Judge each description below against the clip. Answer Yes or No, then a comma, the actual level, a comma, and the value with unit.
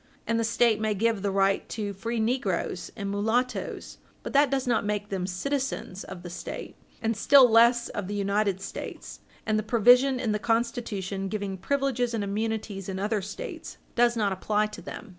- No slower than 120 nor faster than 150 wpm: No, average, 185 wpm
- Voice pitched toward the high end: Yes, high, 215 Hz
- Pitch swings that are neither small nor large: Yes, average, 3.1 semitones